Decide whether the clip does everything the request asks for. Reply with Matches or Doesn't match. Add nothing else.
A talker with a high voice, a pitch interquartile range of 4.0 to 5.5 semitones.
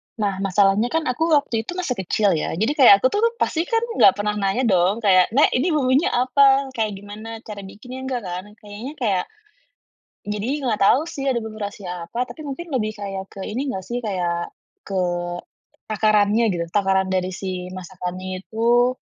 Matches